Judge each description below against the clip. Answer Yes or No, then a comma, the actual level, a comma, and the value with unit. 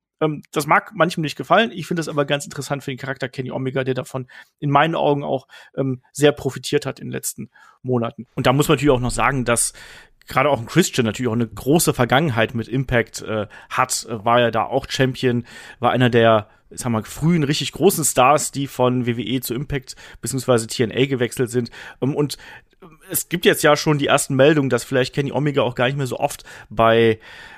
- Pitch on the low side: Yes, low, 130 Hz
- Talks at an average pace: No, fast, 205 wpm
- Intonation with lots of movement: No, average, 3.0 semitones